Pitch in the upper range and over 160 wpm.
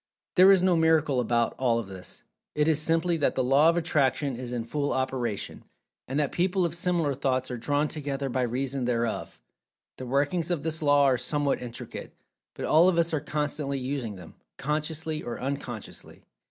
No: medium, 140 Hz; average, 180 wpm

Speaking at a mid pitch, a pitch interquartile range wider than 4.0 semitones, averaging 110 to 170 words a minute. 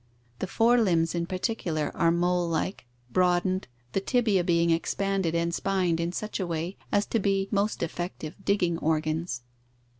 No: medium, 175 Hz; average, 2.8 semitones; average, 150 wpm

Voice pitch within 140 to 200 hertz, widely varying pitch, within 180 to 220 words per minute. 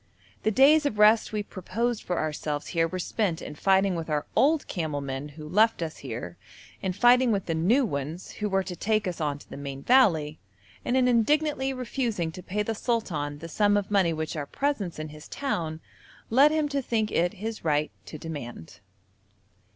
Yes: medium, 185 Hz; wide, 6.7 semitones; average, 195 wpm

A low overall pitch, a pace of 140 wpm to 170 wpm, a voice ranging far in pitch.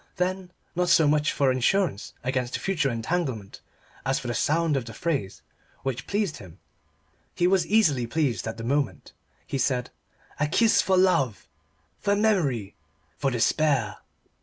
No: medium, 145 Hz; average, 150 wpm; wide, 6.6 semitones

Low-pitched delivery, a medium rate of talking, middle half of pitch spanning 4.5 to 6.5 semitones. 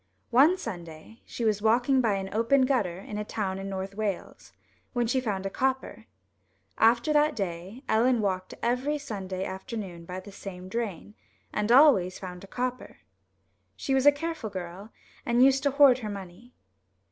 No: high, 220 Hz; average, 170 wpm; average, 5.0 semitones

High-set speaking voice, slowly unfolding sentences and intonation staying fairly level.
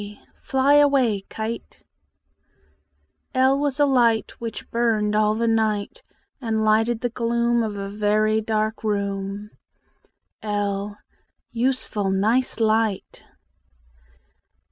Yes: high, 220 Hz; slow, 105 wpm; narrow, 2.2 semitones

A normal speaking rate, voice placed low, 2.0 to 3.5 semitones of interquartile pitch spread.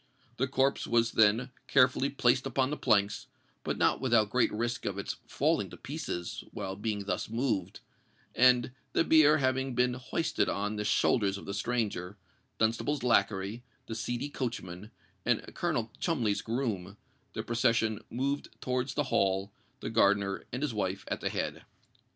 No: average, 155 wpm; low, 115 Hz; average, 4.0 semitones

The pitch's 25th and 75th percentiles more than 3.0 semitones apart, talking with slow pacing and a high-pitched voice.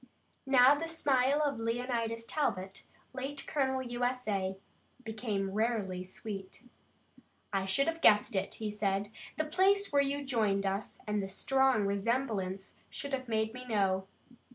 No: average, 5.2 semitones; average, 150 wpm; high, 230 Hz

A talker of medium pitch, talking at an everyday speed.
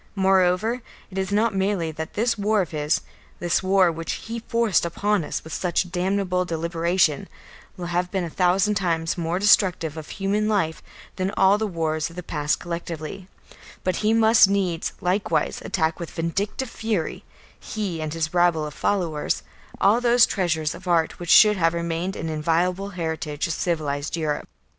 Yes: medium, 180 Hz; average, 170 wpm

